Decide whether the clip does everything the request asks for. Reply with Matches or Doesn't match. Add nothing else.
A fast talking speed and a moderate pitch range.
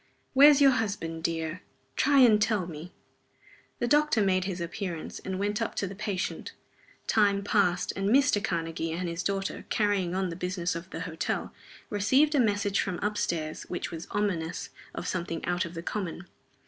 Doesn't match